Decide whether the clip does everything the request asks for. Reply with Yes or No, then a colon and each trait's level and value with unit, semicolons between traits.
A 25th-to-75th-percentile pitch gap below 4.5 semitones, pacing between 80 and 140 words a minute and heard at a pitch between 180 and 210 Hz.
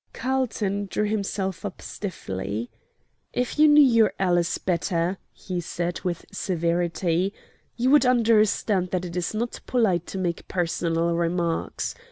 Yes: average, 4.0 semitones; slow, 135 wpm; medium, 185 Hz